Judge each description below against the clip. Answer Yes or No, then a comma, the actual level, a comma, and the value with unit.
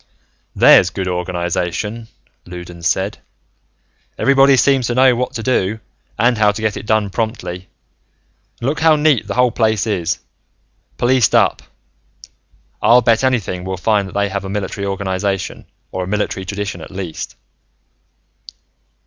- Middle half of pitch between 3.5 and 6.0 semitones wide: Yes, average, 4.2 semitones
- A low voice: Yes, low, 105 Hz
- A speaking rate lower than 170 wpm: Yes, average, 145 wpm